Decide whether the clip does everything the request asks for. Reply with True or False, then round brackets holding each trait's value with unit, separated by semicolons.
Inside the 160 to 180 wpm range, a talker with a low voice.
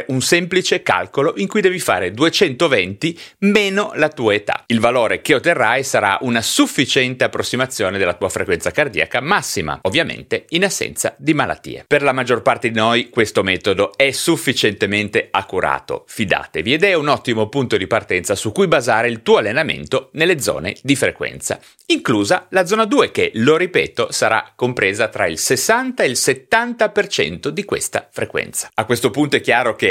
False (165 wpm; 190 Hz)